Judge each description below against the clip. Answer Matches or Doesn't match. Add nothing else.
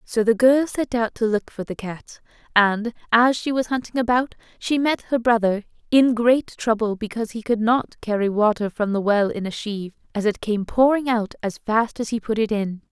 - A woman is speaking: Matches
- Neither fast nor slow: Doesn't match